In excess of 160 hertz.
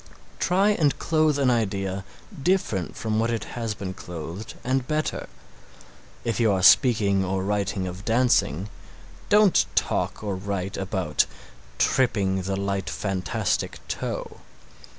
No: low, 100 Hz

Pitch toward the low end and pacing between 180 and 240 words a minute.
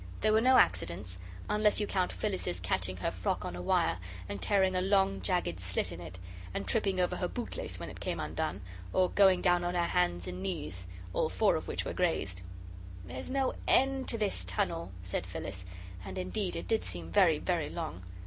Yes: low, 105 Hz; average, 200 wpm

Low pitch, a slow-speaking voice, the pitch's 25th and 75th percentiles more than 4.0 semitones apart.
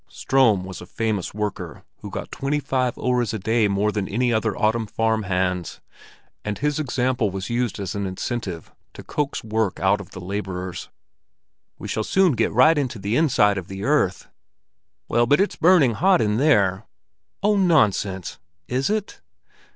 No: low, 110 Hz; average, 165 wpm; average, 5.2 semitones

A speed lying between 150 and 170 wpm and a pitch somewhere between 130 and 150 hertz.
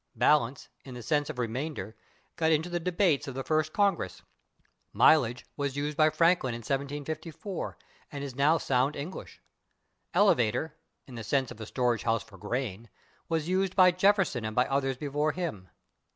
Yes: average, 165 wpm; medium, 140 Hz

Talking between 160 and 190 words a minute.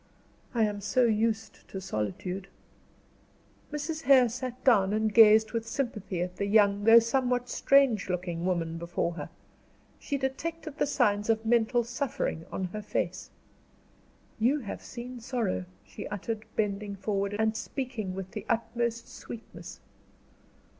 No: average, 140 wpm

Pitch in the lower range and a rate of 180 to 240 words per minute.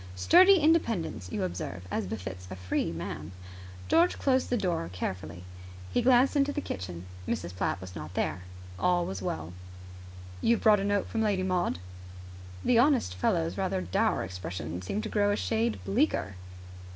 No: low, 100 Hz; average, 165 wpm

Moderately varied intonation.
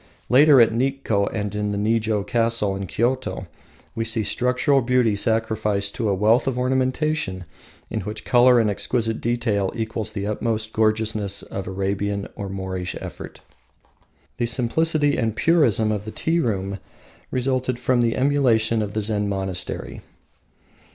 Yes: average, 3.6 semitones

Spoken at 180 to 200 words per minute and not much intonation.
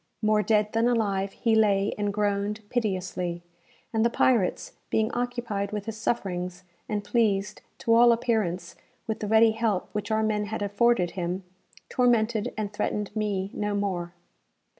No: average, 155 wpm; narrow, 2.1 semitones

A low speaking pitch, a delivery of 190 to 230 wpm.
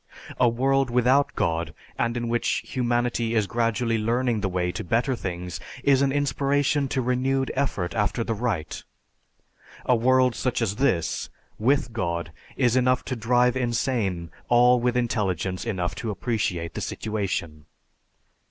No: low, 120 Hz; average, 145 wpm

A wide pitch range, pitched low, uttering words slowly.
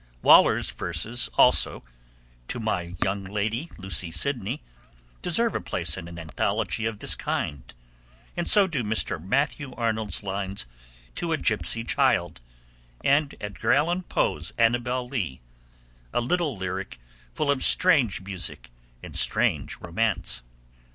Yes: wide, 5.9 semitones; low, 110 Hz; slow, 130 wpm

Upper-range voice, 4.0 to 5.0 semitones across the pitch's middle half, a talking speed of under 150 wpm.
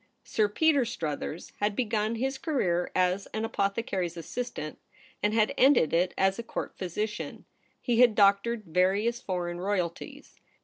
Yes: high, 205 Hz; average, 4.3 semitones; average, 140 wpm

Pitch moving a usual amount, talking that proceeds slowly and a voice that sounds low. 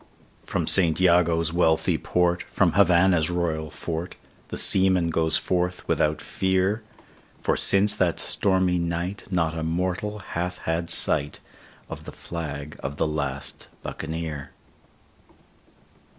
No: narrow, 2.3 semitones; slow, 120 wpm; very low, 85 Hz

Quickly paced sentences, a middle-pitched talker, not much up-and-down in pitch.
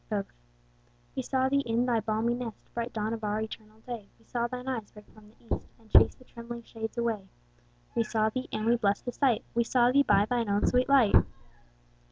No: fast, 220 wpm; high, 230 Hz; narrow, 2.3 semitones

